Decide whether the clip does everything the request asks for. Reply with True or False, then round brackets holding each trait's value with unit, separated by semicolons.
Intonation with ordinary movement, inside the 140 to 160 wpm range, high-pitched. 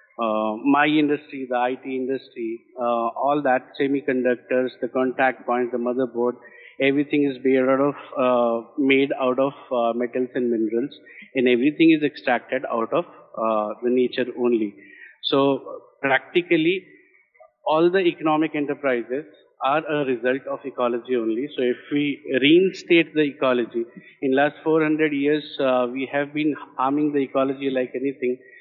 False (3.0 semitones; 145 wpm; 135 Hz)